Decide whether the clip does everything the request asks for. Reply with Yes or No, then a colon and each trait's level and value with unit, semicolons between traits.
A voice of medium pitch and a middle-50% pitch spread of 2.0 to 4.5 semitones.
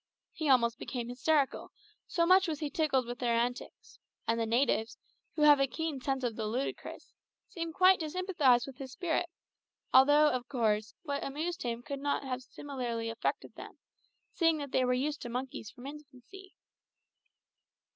No: very high, 270 Hz; average, 3.9 semitones